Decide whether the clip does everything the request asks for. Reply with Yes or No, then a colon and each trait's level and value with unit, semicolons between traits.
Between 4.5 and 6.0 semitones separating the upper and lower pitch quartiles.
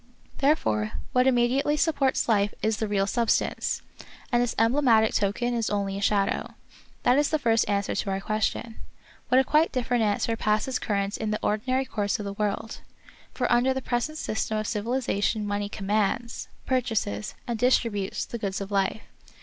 No: average, 3.5 semitones